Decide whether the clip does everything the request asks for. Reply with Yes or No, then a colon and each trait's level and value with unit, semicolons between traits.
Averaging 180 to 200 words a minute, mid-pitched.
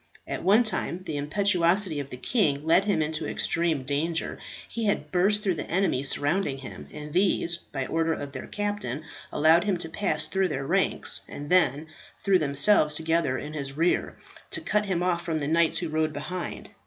Yes: average, 190 wpm; medium, 165 Hz